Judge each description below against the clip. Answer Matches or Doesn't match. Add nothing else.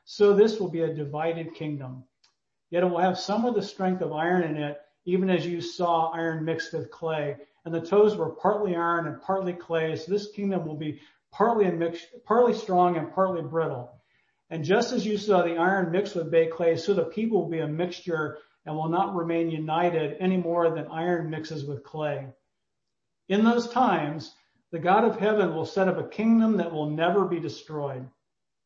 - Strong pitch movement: Doesn't match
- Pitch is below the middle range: Doesn't match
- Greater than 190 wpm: Matches